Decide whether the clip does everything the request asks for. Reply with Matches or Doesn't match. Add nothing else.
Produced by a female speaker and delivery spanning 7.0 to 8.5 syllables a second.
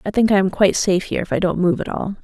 Matches